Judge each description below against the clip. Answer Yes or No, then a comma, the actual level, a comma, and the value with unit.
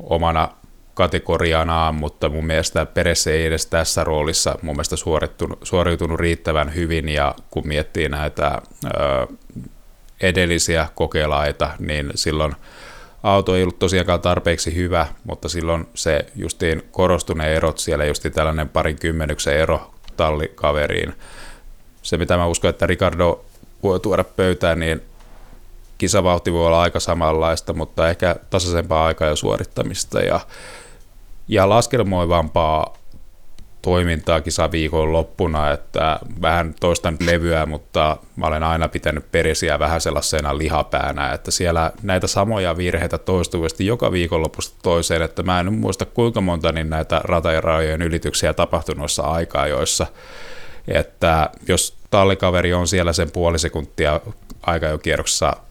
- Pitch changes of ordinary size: No, narrow, 1.9 semitones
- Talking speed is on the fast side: No, average, 125 wpm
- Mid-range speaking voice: No, very low, 85 Hz